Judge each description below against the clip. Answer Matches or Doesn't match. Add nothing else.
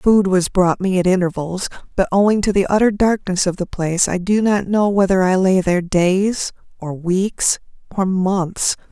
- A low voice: Doesn't match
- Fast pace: Doesn't match